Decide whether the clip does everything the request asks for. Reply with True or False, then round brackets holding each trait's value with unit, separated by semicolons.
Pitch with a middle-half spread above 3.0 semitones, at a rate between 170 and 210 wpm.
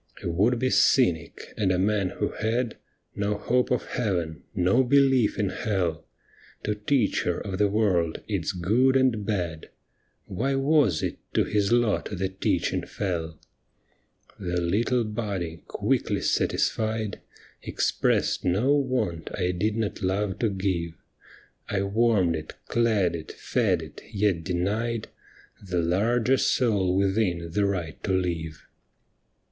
False (4.3 semitones; 140 wpm)